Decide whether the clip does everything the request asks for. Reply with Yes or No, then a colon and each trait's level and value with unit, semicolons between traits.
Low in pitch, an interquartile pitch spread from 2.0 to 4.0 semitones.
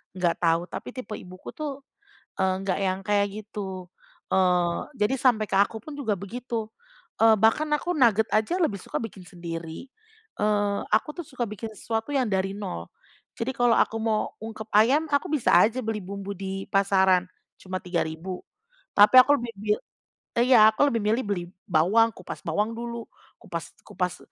No: high, 210 Hz; average, 3.7 semitones